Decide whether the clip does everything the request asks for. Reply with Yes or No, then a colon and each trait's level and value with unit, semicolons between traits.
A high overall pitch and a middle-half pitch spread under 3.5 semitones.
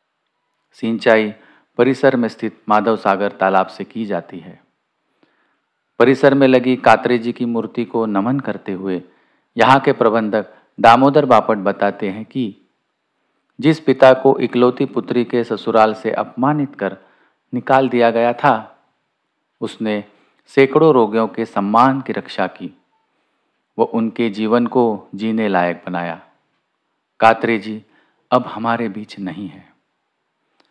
No: low, 115 Hz; average, 2.7 semitones